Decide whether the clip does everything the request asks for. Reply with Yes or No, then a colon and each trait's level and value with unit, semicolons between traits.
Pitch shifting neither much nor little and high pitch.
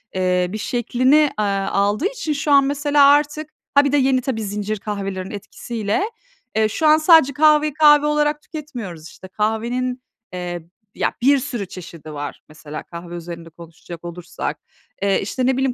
No: wide, 7.8 semitones; high, 235 Hz